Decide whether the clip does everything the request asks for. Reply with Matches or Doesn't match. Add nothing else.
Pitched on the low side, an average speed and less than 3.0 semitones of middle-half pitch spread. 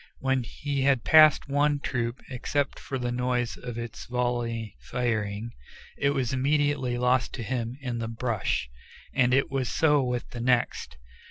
Matches